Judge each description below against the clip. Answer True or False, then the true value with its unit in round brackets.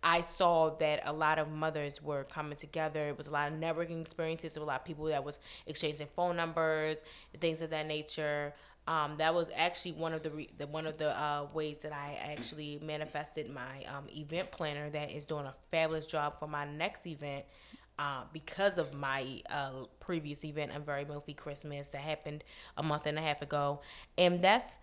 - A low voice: False (150 Hz)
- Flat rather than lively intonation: True (1.5 semitones)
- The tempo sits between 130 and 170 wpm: False (205 wpm)